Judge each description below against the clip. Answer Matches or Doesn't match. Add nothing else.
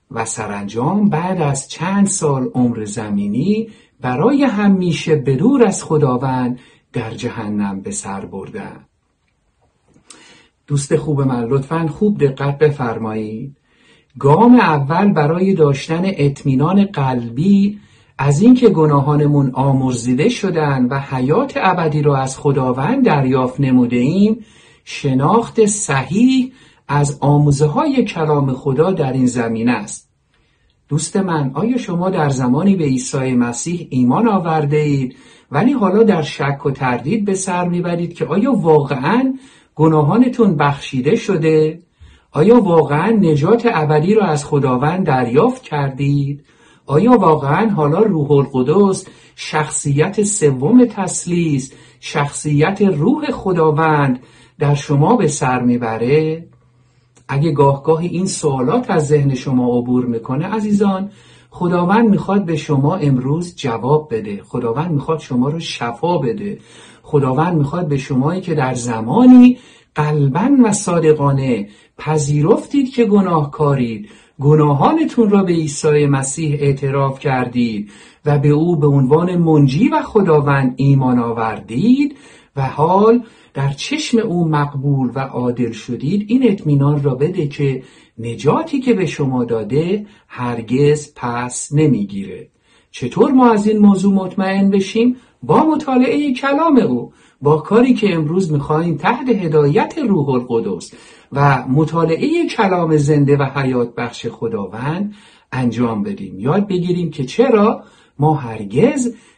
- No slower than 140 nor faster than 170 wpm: Doesn't match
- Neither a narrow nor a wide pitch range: Doesn't match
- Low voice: Doesn't match